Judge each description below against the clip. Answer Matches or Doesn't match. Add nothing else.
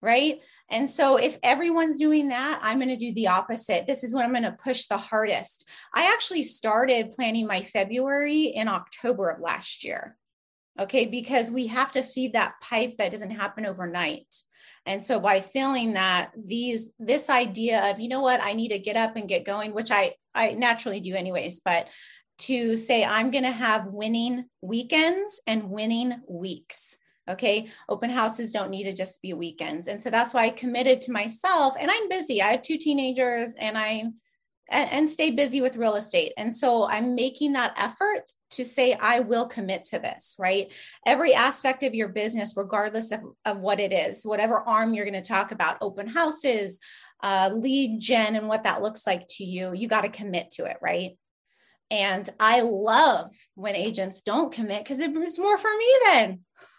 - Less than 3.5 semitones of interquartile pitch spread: Doesn't match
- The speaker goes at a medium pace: Matches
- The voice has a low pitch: Doesn't match